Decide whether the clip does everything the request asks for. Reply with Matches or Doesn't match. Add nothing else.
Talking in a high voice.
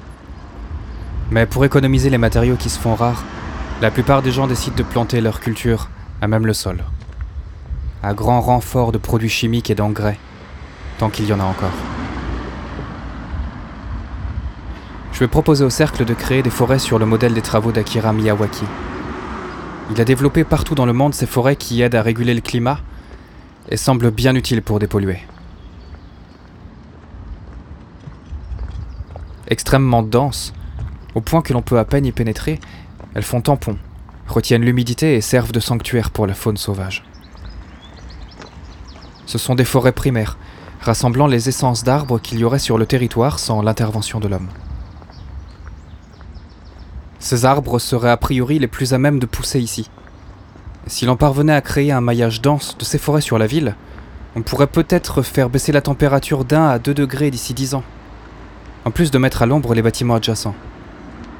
Doesn't match